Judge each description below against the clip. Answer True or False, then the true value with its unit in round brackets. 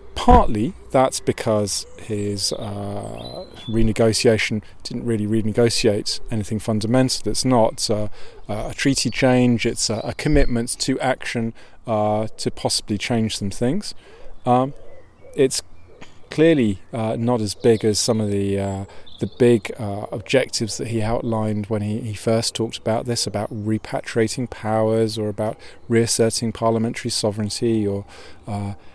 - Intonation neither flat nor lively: False (2.0 semitones)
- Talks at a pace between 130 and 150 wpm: True (135 wpm)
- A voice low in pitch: True (110 Hz)